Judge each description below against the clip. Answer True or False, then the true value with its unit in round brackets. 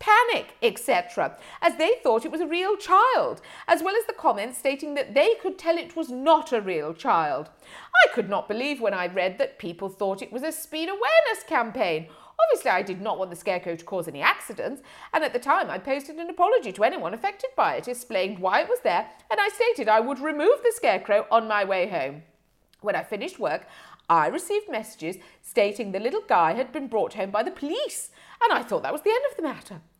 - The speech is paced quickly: True (220 wpm)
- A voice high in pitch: True (285 Hz)